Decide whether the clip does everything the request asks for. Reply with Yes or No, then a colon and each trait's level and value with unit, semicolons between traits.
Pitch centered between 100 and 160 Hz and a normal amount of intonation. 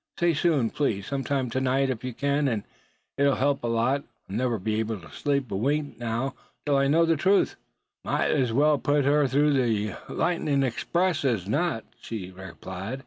Yes: low, 135 Hz; average, 4.2 semitones